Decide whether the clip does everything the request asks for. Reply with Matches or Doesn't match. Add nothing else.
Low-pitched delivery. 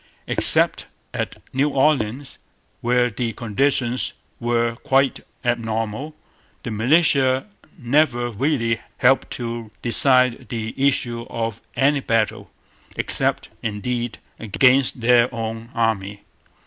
Matches